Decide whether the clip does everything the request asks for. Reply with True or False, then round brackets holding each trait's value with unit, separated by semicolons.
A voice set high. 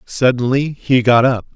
False (125 Hz)